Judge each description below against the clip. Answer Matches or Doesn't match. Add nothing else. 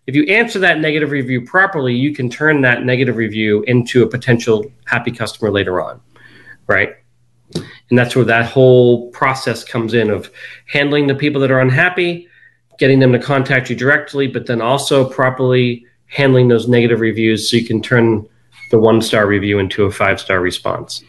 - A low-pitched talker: Matches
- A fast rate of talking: Doesn't match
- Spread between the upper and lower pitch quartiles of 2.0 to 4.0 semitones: Matches